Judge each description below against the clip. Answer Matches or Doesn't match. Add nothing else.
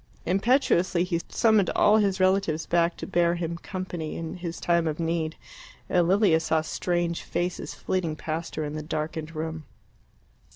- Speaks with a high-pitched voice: Doesn't match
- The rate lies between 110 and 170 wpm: Matches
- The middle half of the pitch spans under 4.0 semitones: Matches